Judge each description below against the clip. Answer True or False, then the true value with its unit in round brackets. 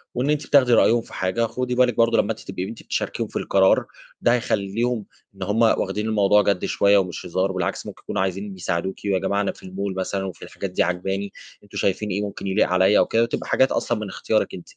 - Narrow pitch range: False (3.1 semitones)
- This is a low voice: True (100 Hz)